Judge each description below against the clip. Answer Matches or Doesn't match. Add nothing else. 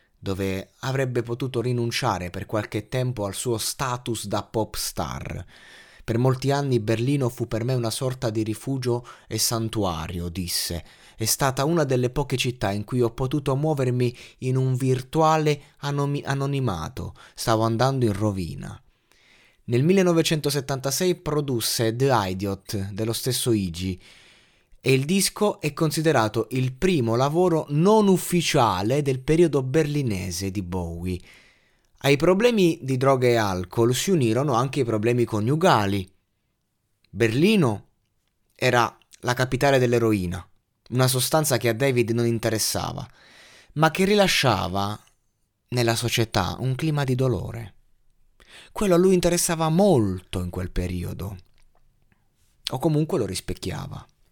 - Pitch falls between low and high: Doesn't match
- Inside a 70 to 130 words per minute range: Matches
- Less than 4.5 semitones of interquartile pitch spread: Doesn't match